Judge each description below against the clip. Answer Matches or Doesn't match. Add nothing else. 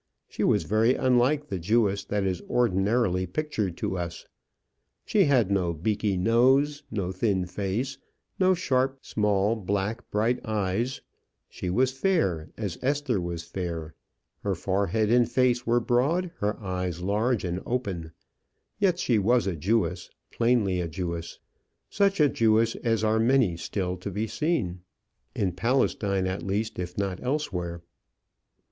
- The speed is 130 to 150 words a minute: Matches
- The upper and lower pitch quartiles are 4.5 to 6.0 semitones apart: Matches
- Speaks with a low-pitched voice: Matches